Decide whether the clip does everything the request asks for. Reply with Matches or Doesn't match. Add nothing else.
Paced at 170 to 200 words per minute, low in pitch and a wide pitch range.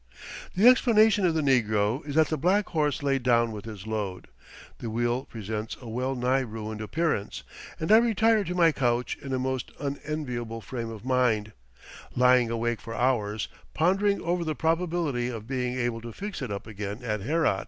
Matches